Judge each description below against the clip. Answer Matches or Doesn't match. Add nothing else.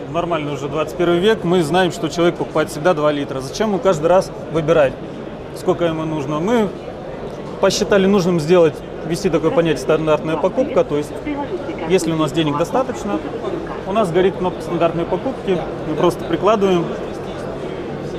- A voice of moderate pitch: Matches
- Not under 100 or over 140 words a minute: Doesn't match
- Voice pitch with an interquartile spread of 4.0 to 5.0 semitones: Doesn't match